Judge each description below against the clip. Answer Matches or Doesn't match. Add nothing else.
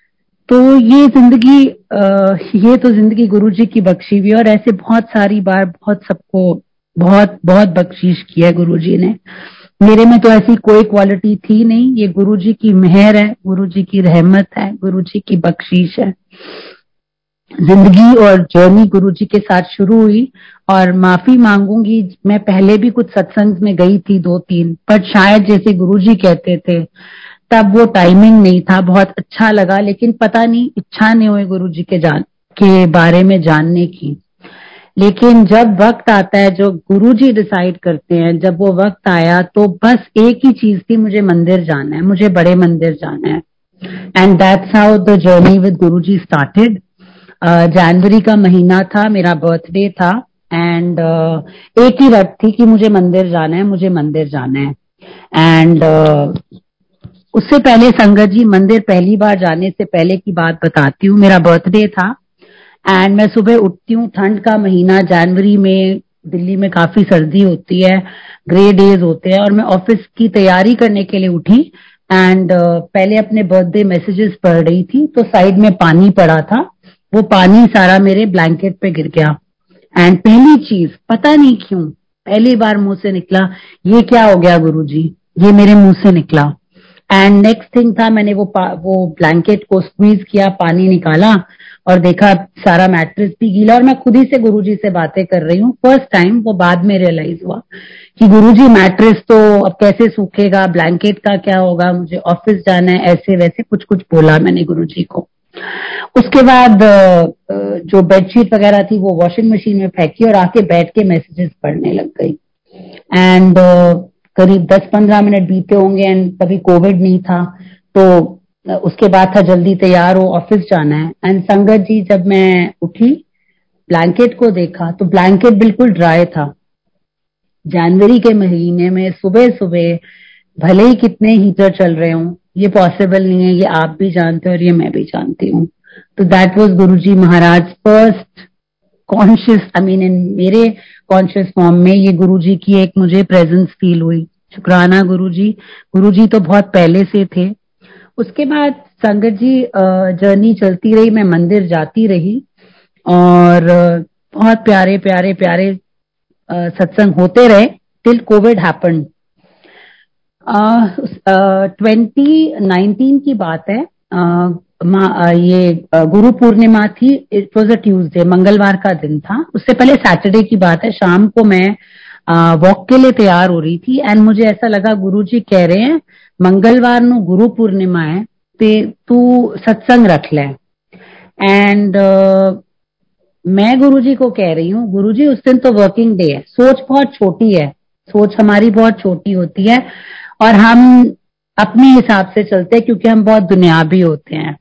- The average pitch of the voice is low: Doesn't match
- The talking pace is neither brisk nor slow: Matches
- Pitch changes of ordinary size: Matches